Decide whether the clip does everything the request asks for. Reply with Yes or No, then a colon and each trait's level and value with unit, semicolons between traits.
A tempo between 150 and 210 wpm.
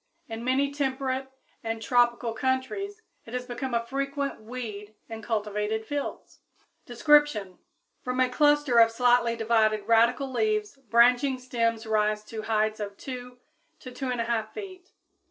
No: slow, 135 wpm